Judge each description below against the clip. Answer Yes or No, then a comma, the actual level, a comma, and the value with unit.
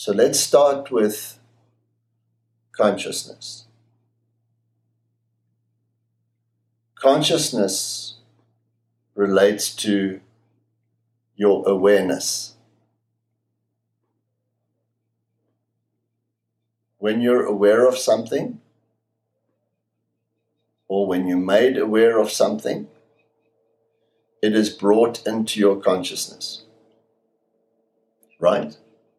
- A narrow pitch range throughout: Yes, narrow, 0.6 semitones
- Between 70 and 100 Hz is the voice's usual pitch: No, low, 115 Hz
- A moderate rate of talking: No, slow, 60 wpm